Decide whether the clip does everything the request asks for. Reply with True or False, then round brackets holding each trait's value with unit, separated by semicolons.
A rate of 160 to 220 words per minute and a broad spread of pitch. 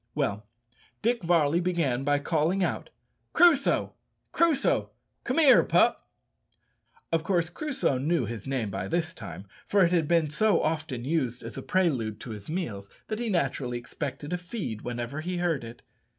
True (165 wpm; 6.3 semitones)